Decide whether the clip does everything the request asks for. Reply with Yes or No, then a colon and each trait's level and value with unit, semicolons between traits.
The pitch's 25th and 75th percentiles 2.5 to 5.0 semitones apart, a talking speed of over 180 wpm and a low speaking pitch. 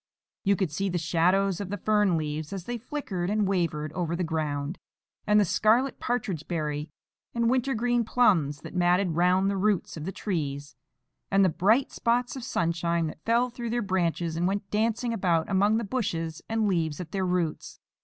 No: average, 4.6 semitones; average, 190 wpm; high, 190 Hz